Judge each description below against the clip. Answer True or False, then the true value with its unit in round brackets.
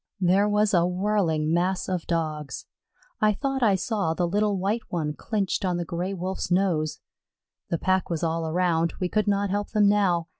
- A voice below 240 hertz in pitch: True (185 Hz)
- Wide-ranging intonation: False (3.3 semitones)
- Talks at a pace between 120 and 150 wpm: False (185 wpm)